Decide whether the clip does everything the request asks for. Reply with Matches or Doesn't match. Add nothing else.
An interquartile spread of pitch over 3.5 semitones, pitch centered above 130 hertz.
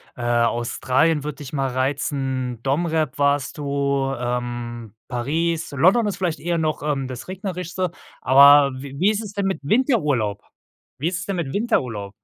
Matches